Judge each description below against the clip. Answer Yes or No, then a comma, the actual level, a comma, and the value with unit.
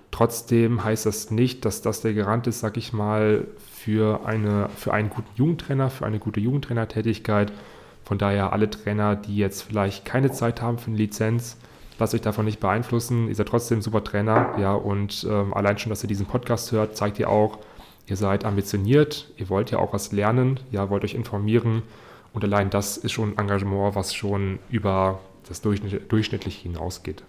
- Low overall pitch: Yes, low, 110 Hz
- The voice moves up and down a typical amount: No, narrow, 2.3 semitones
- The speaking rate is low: No, fast, 190 wpm